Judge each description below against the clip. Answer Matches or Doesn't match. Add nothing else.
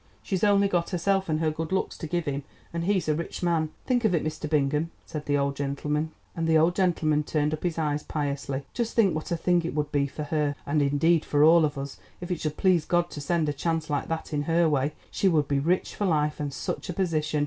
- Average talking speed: Doesn't match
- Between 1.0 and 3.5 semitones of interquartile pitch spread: Matches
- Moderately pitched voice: Matches